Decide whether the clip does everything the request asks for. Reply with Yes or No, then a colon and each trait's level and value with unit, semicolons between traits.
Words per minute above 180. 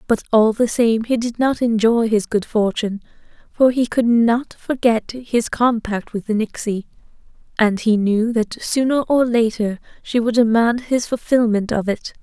No: average, 170 wpm